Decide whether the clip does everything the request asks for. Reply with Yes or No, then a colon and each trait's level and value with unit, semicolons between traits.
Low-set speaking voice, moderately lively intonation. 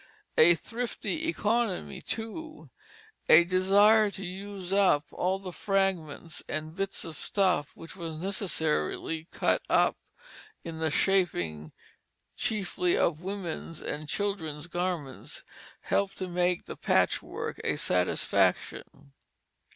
No: medium, 180 Hz; average, 3.7 semitones